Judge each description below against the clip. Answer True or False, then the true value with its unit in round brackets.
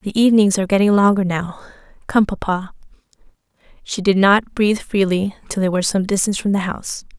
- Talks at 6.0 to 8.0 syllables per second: True (6.2 syllables/s)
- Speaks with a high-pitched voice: True (195 Hz)